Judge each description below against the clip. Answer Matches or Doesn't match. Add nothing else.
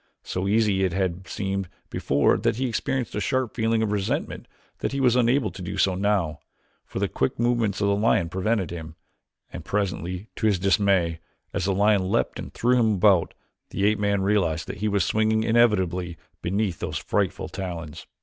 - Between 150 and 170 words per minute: Doesn't match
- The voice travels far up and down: Doesn't match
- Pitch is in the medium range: Doesn't match